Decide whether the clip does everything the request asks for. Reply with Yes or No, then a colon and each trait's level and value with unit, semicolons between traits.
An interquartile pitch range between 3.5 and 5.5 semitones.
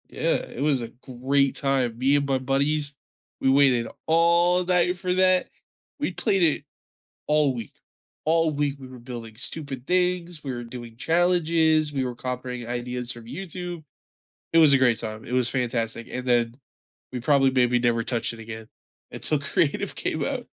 Yes: average, 4.8 semitones